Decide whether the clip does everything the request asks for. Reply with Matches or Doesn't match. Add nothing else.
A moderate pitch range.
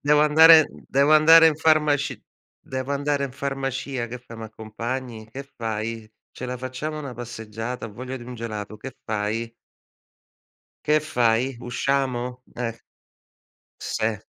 Matches